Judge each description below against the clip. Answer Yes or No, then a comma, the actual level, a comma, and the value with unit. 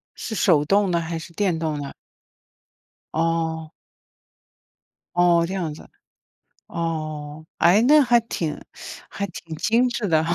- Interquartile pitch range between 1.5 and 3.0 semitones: No, average, 3.9 semitones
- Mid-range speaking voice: Yes, medium, 170 Hz